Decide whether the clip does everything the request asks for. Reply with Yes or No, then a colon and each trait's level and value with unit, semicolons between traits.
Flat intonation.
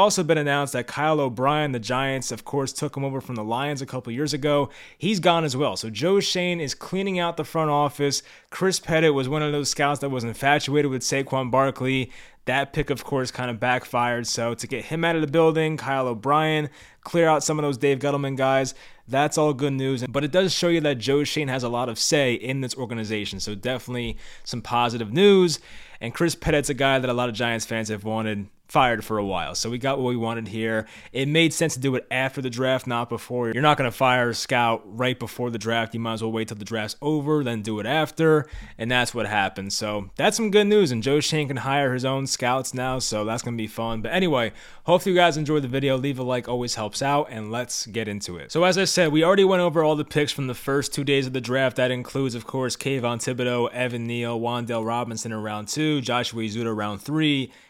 No: average, 4.0 semitones